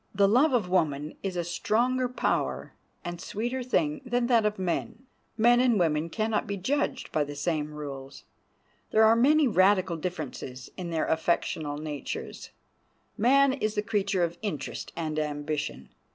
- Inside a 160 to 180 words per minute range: Yes, average, 165 wpm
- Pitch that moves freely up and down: Yes, wide, 7.3 semitones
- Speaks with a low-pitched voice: No, high, 190 Hz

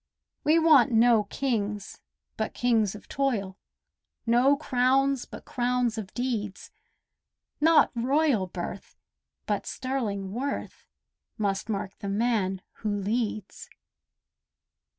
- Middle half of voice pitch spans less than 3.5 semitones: No, average, 4.3 semitones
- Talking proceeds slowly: Yes, slow, 105 wpm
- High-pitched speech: Yes, high, 230 Hz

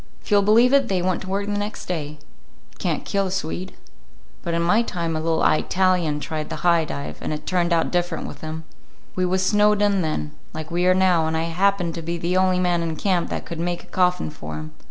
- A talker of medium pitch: Yes, medium, 175 Hz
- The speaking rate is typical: No, fast, 240 wpm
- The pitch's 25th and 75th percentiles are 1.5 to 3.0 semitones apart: Yes, narrow, 2.6 semitones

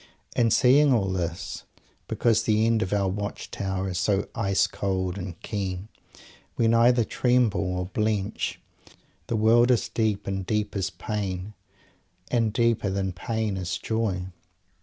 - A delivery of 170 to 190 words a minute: No, average, 150 wpm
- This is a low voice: Yes, low, 105 Hz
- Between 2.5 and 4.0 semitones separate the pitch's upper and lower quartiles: Yes, average, 3.2 semitones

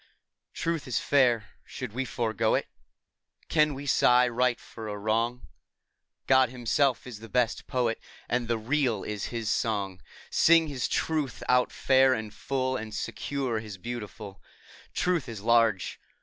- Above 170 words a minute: No, average, 150 wpm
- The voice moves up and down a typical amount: Yes, average, 3.1 semitones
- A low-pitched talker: Yes, low, 120 Hz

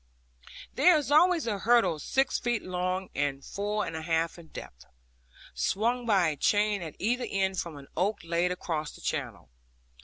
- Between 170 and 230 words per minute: Yes, average, 175 wpm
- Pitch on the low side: No, high, 190 Hz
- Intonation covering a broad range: Yes, wide, 5.8 semitones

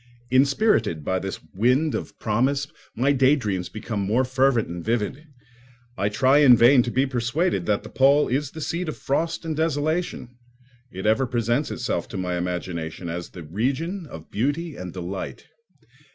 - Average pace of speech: Yes, average, 165 wpm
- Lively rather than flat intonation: Yes, wide, 6.6 semitones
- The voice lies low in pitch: Yes, low, 125 Hz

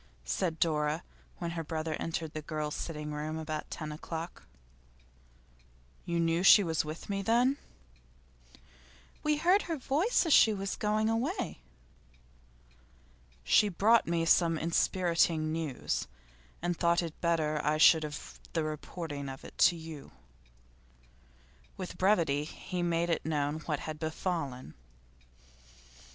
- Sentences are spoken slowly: Yes, slow, 130 wpm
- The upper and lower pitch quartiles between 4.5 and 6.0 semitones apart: No, average, 3.1 semitones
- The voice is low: No, medium, 165 Hz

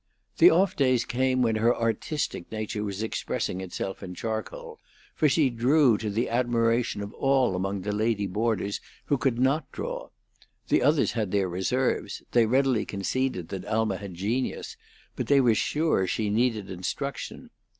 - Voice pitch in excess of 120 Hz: No, low, 115 Hz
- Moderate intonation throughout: Yes, average, 4.2 semitones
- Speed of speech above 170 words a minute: No, average, 160 wpm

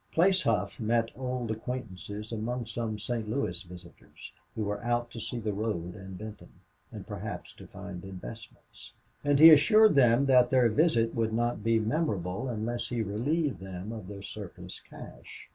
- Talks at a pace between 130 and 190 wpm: Yes, average, 170 wpm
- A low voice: Yes, low, 115 Hz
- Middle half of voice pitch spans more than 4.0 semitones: No, average, 3.3 semitones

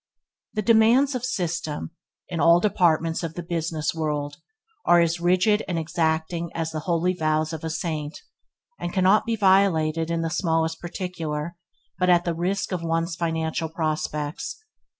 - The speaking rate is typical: Yes, average, 155 wpm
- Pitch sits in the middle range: Yes, medium, 165 Hz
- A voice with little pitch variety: Yes, narrow, 2.3 semitones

